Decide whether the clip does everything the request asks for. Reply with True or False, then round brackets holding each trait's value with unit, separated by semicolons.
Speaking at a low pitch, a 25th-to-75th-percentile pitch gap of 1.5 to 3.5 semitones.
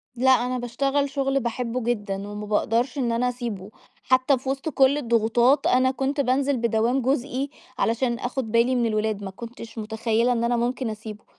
False (245 Hz; 2.6 semitones)